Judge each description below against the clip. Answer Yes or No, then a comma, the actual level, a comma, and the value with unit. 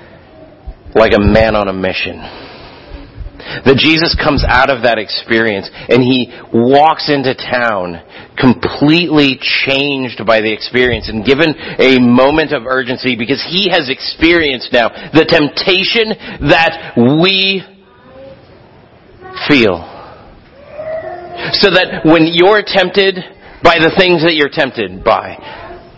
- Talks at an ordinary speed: No, slow, 120 wpm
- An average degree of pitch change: No, wide, 6.8 semitones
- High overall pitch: No, medium, 145 Hz